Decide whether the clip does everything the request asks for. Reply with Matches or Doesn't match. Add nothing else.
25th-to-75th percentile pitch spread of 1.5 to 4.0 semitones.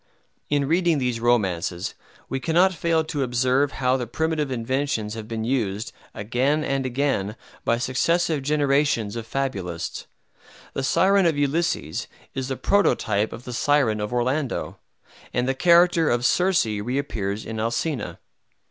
Doesn't match